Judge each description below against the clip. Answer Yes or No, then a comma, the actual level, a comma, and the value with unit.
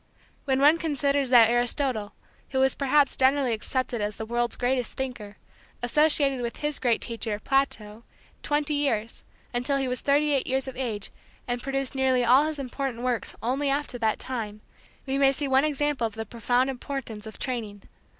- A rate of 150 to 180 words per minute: Yes, average, 175 wpm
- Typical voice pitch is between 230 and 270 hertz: Yes, very high, 260 Hz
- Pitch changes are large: No, average, 2.9 semitones